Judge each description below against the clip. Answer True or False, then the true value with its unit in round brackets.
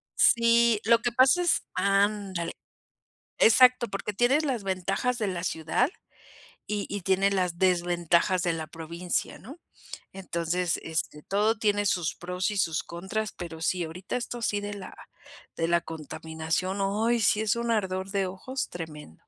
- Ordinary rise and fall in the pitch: True (4.2 semitones)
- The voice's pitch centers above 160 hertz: True (190 Hz)